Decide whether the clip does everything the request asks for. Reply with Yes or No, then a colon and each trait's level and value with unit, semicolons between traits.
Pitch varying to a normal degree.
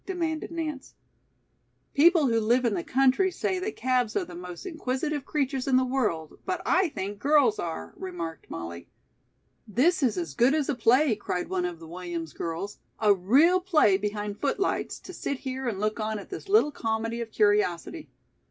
No: wide, 7.7 semitones